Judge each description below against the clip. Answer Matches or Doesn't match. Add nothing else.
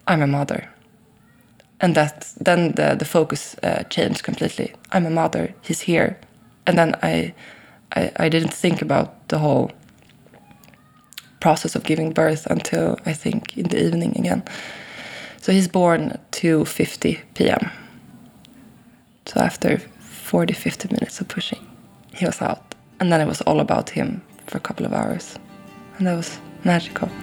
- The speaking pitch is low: Doesn't match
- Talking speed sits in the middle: Matches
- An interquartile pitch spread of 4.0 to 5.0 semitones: Doesn't match